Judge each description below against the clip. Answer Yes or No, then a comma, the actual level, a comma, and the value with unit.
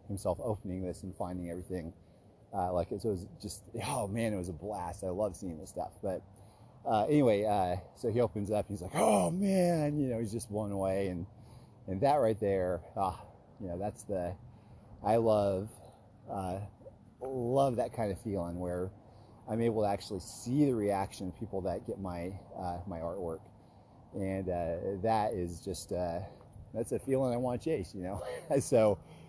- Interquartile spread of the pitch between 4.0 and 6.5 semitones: No, average, 3.6 semitones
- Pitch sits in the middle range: No, low, 100 Hz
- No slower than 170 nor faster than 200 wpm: Yes, average, 190 wpm